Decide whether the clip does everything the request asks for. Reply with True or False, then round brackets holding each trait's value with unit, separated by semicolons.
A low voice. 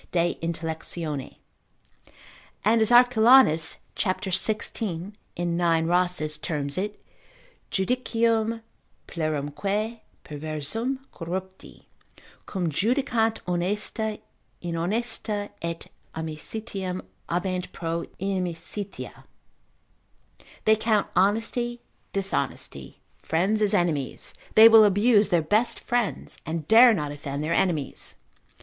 False (190 Hz)